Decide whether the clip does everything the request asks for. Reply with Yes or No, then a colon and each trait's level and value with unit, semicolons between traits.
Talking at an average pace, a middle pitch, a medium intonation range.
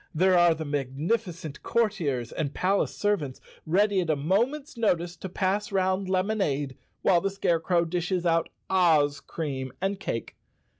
Yes: average, 145 wpm; medium, 175 Hz; average, 4.2 semitones